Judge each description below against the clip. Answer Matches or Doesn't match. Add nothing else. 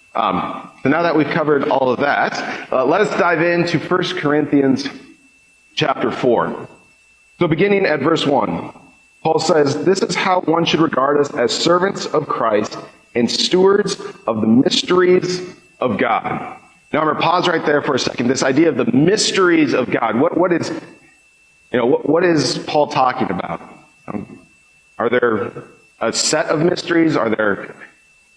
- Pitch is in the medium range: Matches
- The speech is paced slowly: Doesn't match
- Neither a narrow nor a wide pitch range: Matches